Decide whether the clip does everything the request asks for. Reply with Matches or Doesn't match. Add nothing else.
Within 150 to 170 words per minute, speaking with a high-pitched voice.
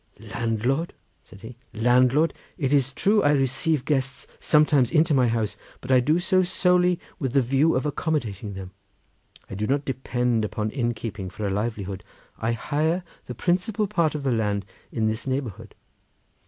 Doesn't match